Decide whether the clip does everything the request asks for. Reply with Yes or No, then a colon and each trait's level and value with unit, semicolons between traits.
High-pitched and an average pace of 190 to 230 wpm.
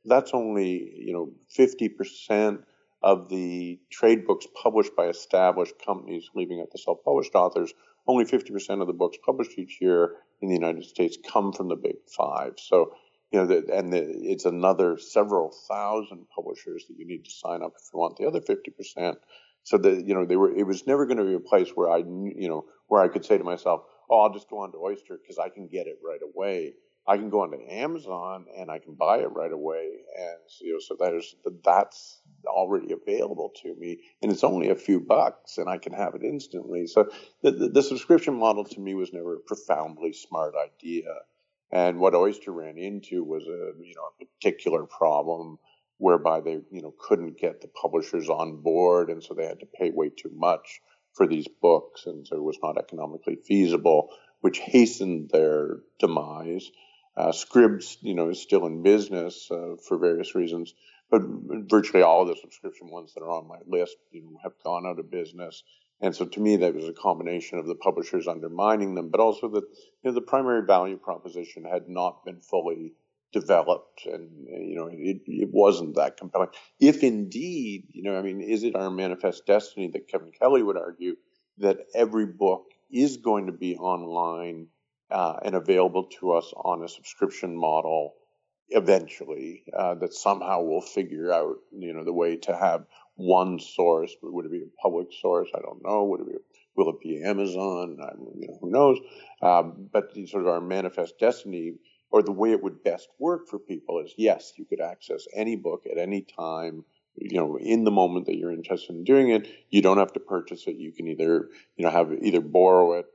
Yes: very high, 345 Hz; average, 200 wpm